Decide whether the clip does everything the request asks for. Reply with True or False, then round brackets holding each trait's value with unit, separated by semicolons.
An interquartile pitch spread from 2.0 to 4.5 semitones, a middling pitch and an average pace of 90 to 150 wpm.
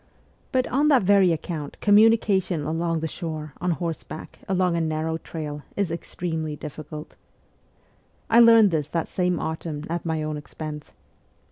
True (3.5 semitones; 165 Hz; 145 wpm)